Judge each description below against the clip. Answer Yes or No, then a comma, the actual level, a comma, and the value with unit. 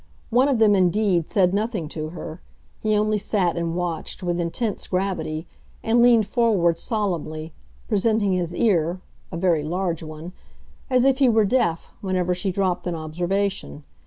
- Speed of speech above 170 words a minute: No, average, 160 wpm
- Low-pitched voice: No, medium, 185 Hz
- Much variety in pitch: No, average, 4.1 semitones